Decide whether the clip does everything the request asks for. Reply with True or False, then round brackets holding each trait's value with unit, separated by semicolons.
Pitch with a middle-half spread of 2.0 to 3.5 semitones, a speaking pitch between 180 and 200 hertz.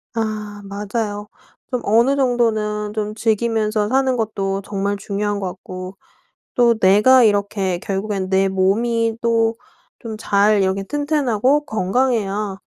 False (2.7 semitones; 210 Hz)